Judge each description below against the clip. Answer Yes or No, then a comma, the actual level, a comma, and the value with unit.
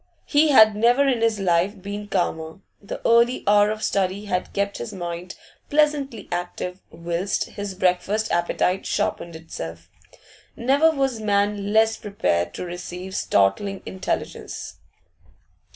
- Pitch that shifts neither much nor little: Yes, average, 3.8 semitones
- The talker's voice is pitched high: Yes, high, 200 Hz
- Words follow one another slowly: Yes, slow, 130 wpm